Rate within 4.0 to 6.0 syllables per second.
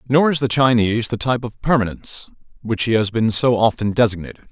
No: 6.4 syllables/s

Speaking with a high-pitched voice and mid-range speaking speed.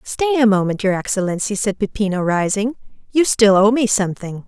Yes: high, 210 Hz; average, 175 wpm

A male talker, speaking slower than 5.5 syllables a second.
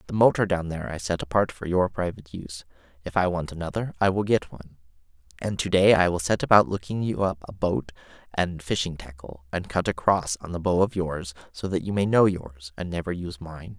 No: male; 5.7 syllables/s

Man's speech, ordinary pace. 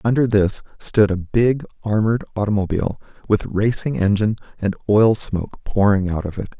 Yes: male; average, 155 wpm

